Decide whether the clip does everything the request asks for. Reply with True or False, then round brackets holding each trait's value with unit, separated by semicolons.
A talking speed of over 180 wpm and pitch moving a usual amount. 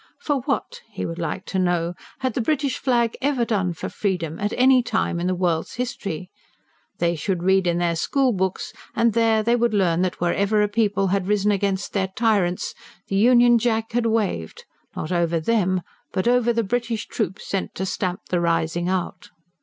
True (190 wpm; 4.6 semitones)